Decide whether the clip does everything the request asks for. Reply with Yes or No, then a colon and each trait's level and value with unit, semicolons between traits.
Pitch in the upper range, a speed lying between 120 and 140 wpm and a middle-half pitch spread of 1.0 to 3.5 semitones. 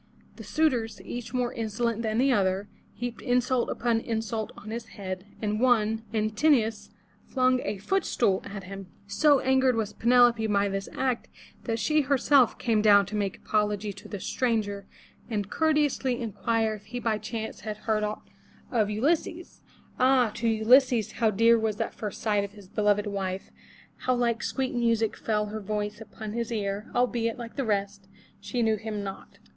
No: high, 220 Hz; average, 180 wpm; average, 2.8 semitones